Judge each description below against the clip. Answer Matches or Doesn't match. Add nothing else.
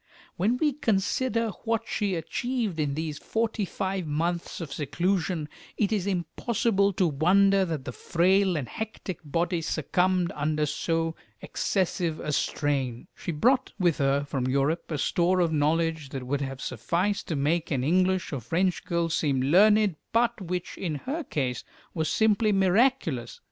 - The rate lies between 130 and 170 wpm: Matches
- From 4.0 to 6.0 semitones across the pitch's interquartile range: Matches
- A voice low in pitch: Doesn't match